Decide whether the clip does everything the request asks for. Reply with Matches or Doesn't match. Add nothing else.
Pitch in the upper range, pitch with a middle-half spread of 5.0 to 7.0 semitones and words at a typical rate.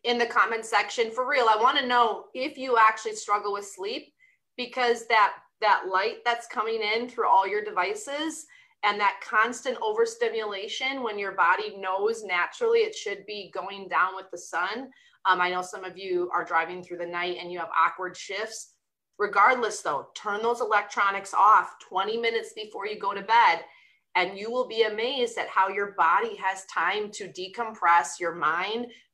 Matches